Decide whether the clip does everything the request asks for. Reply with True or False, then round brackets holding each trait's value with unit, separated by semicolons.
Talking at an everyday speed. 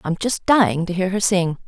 False (250 wpm)